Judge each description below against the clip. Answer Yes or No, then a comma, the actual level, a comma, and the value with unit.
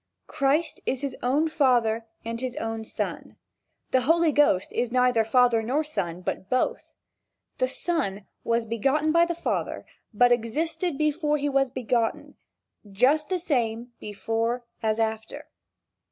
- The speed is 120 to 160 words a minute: Yes, average, 140 wpm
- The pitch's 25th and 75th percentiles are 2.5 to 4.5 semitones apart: No, average, 4.9 semitones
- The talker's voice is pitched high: Yes, very high, 250 Hz